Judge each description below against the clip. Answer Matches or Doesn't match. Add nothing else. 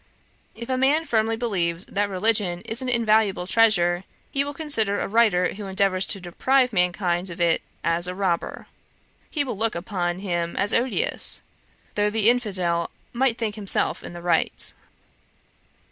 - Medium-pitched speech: Doesn't match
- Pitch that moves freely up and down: Doesn't match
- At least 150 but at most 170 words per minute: Matches